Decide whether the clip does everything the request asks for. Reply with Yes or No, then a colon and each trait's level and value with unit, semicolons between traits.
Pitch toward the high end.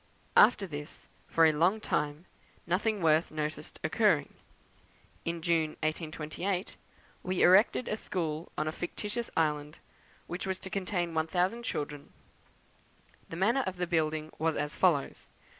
No: medium, 165 Hz